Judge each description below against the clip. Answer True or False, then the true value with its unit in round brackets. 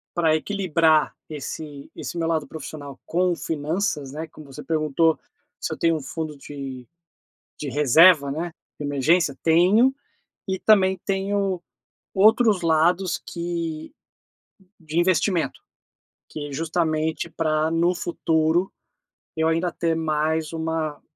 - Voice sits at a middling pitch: True (160 Hz)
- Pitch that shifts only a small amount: True (2.3 semitones)